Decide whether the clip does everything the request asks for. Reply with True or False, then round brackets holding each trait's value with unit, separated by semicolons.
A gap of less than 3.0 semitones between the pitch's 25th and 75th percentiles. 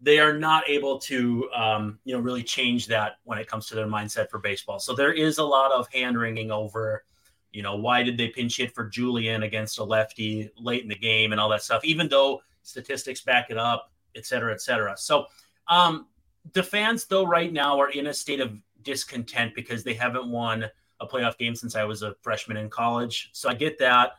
False (3.8 semitones)